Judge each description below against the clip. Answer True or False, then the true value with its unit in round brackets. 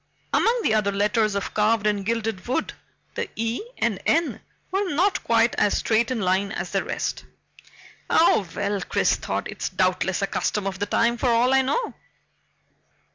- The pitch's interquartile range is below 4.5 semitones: True (3.6 semitones)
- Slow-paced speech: False (175 wpm)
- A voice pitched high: True (220 Hz)